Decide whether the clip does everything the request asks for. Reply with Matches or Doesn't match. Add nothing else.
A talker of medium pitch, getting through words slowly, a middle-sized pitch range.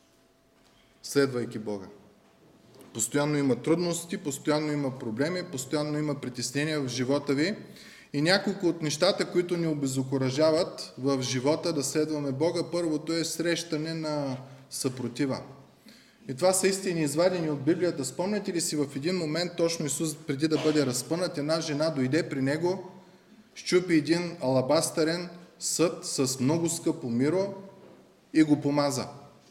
Doesn't match